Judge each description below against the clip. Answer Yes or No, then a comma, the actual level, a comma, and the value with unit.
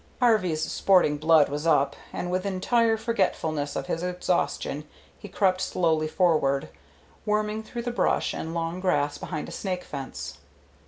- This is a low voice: No, medium, 180 Hz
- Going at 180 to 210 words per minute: No, average, 150 wpm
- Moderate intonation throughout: Yes, average, 4.3 semitones